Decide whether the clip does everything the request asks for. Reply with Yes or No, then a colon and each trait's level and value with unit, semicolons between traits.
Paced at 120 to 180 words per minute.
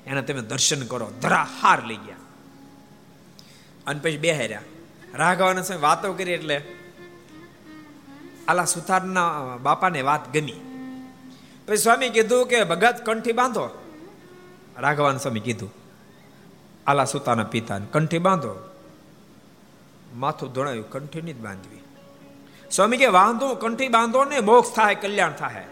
No: average, 105 wpm